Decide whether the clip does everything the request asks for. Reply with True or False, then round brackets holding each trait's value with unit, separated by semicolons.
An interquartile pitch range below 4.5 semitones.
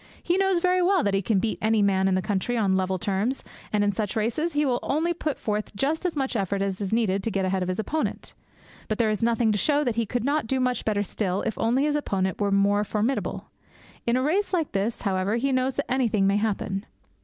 False (5.3 semitones)